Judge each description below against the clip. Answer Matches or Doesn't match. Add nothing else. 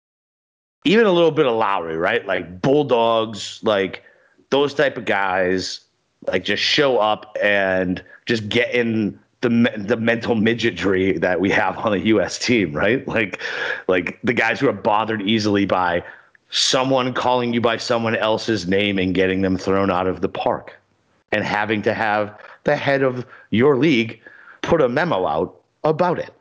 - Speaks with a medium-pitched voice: Doesn't match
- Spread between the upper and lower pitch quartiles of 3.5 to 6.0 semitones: Matches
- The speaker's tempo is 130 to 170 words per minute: Matches